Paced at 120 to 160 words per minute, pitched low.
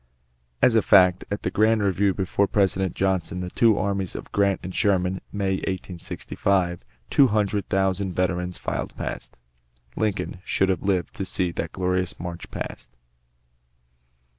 Yes: average, 150 wpm; very low, 95 Hz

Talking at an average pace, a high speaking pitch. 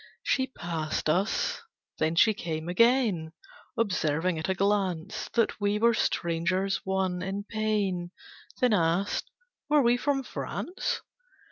No: slow, 125 wpm; high, 195 Hz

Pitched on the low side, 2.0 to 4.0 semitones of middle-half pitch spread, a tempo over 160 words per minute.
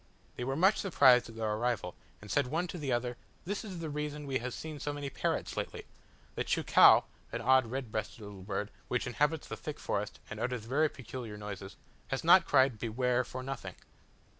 No: low, 130 Hz; average, 4.6 semitones; average, 200 wpm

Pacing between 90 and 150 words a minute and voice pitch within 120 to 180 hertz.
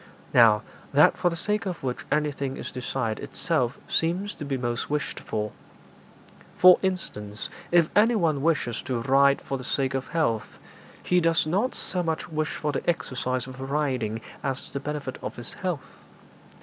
No: average, 165 wpm; medium, 140 Hz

